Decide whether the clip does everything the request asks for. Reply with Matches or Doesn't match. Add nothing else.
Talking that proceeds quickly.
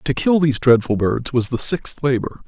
Matches